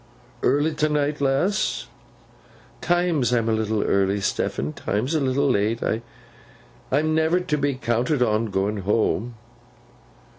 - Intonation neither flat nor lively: No, wide, 5.7 semitones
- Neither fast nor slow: No, slow, 120 wpm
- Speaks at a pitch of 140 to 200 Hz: No, low, 130 Hz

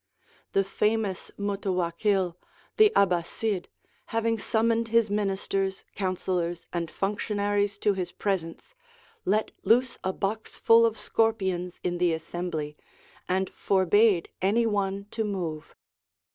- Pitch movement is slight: No, average, 3.2 semitones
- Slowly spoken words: Yes, slow, 115 wpm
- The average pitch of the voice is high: Yes, high, 195 Hz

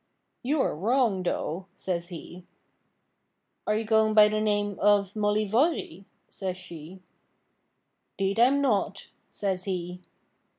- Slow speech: Yes, slow, 125 wpm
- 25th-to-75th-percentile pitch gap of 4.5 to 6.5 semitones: No, average, 2.8 semitones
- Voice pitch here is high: Yes, high, 205 Hz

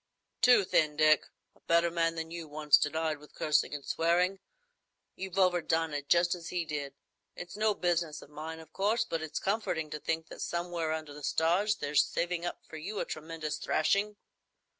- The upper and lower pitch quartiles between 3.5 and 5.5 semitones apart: No, narrow, 2.5 semitones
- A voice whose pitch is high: No, medium, 165 Hz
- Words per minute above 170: Yes, average, 185 wpm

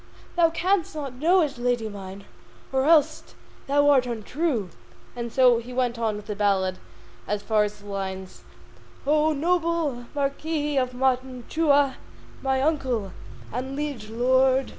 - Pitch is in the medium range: No, very high, 260 Hz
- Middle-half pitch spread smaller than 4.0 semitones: No, average, 4.9 semitones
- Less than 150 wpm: Yes, average, 140 wpm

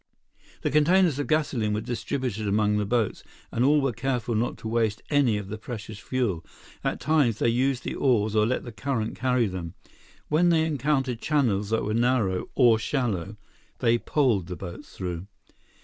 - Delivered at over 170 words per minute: Yes, average, 180 wpm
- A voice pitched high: No, low, 115 Hz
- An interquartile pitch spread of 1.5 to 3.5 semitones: No, average, 4.3 semitones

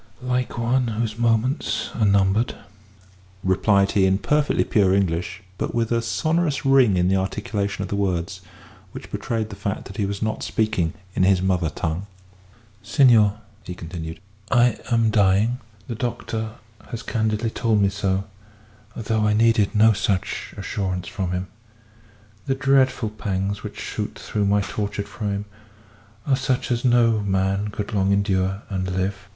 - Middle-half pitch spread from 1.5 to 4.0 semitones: Yes, average, 3.1 semitones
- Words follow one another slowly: No, average, 155 wpm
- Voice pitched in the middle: No, low, 105 Hz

